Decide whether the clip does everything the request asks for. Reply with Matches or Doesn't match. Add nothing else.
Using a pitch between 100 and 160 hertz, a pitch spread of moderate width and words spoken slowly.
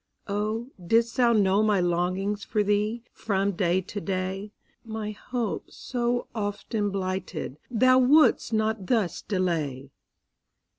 Doesn't match